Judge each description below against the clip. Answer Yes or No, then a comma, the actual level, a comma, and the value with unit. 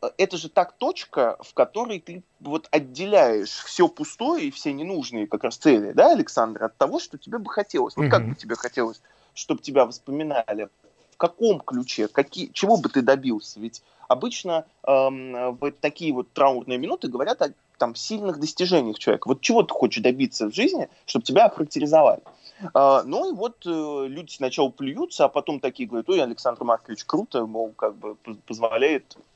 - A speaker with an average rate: No, fast, 175 wpm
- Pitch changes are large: Yes, wide, 8.6 semitones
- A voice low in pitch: No, medium, 150 Hz